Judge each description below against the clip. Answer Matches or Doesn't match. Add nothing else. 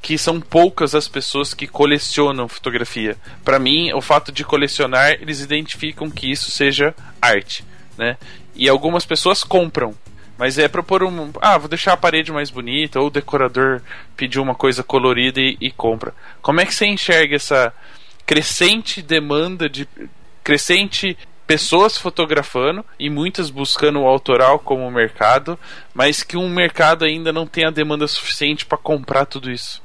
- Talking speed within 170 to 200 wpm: Doesn't match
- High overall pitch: Doesn't match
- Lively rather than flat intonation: Doesn't match